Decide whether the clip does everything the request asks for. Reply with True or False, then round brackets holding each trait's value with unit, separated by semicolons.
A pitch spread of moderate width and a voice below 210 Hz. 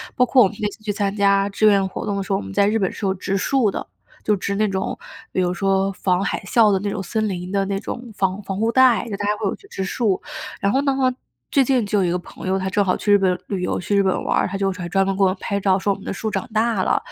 False (1.7 semitones; 200 Hz)